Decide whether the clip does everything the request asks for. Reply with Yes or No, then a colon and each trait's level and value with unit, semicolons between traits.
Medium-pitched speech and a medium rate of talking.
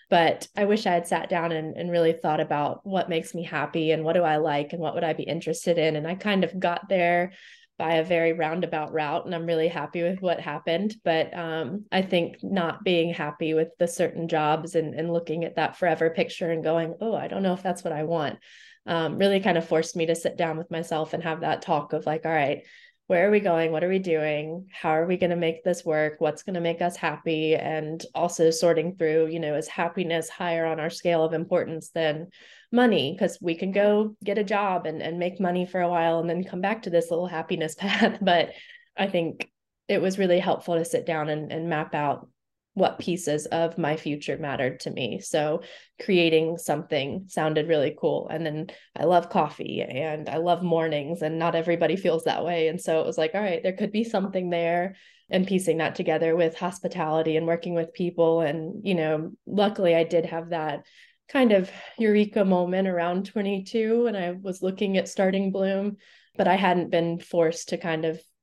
No: medium, 170 Hz; fast, 220 wpm